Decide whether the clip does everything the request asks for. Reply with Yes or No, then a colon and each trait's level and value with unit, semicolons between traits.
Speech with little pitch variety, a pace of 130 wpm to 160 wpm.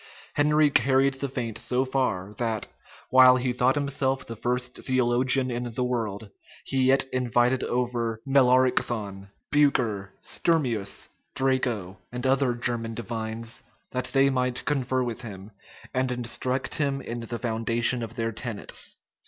Yes: narrow, 2.3 semitones; average, 140 wpm